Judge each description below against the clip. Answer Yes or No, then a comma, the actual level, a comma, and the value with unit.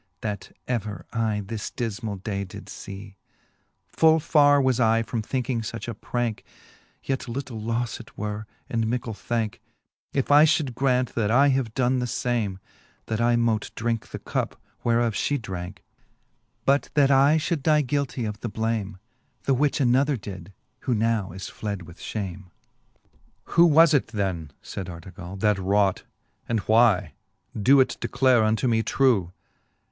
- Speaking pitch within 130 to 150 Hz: No, low, 115 Hz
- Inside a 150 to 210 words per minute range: Yes, average, 160 wpm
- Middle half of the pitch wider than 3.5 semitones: Yes, average, 3.9 semitones